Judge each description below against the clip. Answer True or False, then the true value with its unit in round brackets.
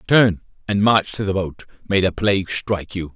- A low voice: True (95 Hz)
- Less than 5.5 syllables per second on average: True (5.2 syllables/s)